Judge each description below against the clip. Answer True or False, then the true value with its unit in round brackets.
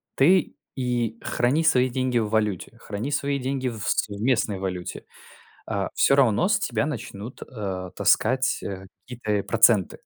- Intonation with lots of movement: False (4.1 semitones)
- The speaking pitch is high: False (115 Hz)